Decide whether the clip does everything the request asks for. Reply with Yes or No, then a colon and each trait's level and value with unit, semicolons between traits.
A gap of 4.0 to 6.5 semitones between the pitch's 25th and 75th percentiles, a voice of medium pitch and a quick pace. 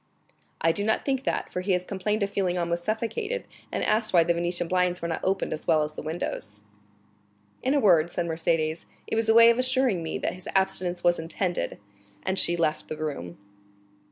Yes: average, 4.3 semitones; medium, 180 Hz; fast, 210 wpm